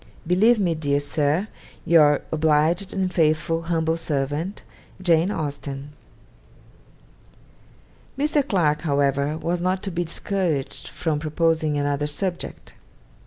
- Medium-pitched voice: Yes, medium, 160 Hz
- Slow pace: Yes, slow, 110 wpm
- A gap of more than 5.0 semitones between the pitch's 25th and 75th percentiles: No, average, 3.3 semitones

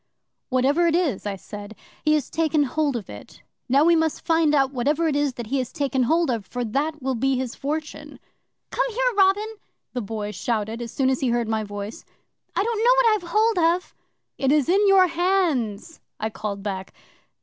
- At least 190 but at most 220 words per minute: Yes, fast, 205 wpm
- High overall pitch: Yes, very high, 280 Hz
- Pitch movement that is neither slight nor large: No, wide, 6.4 semitones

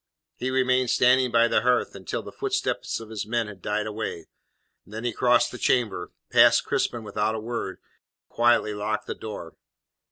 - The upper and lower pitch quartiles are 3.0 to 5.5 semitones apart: No, narrow, 2.5 semitones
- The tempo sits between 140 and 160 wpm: No, average, 180 wpm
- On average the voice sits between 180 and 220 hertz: No, low, 110 Hz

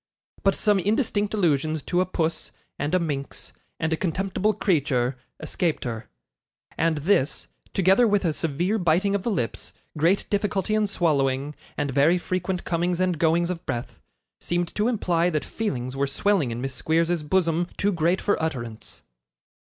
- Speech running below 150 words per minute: No, average, 160 wpm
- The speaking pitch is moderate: Yes, medium, 170 Hz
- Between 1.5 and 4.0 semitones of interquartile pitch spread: No, average, 4.6 semitones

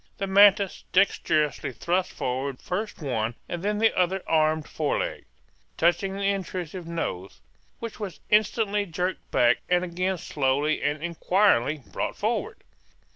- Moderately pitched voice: Yes, medium, 175 Hz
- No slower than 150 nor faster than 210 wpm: No, slow, 135 wpm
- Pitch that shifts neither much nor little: Yes, average, 4.6 semitones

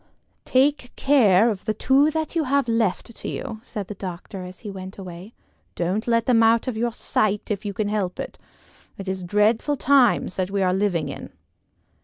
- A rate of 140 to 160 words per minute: No, average, 195 wpm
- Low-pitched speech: No, high, 215 Hz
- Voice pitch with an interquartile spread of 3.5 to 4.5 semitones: Yes, average, 4.1 semitones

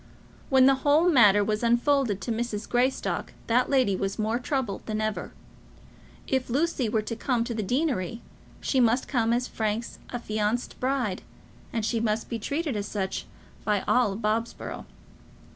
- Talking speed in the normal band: Yes, average, 155 wpm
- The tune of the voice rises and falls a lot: No, average, 3.3 semitones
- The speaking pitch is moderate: No, high, 235 Hz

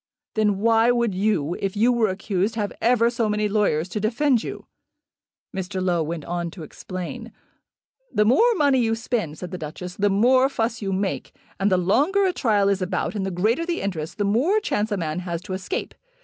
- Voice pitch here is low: No, high, 205 Hz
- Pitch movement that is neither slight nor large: Yes, average, 4.2 semitones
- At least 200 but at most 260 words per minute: Yes, fast, 205 wpm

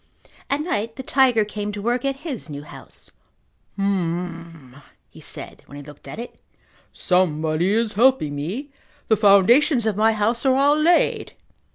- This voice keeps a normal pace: Yes, average, 160 wpm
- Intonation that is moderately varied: No, wide, 7.1 semitones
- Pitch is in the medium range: No, high, 210 Hz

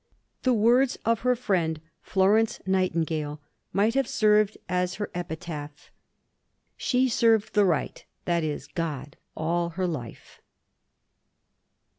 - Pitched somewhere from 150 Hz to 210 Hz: Yes, medium, 185 Hz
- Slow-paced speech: Yes, slow, 110 wpm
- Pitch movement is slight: No, wide, 5.4 semitones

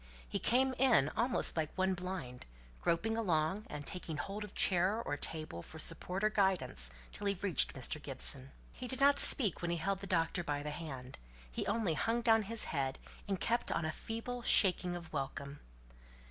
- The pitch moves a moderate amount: No, wide, 6.2 semitones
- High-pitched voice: No, medium, 180 Hz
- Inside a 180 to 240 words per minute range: Yes, average, 190 wpm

